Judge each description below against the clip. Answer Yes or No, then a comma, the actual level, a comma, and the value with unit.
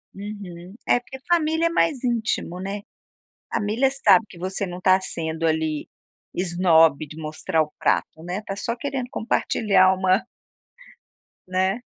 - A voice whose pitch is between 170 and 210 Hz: Yes, high, 190 Hz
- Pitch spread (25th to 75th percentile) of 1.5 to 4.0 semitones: No, average, 5.3 semitones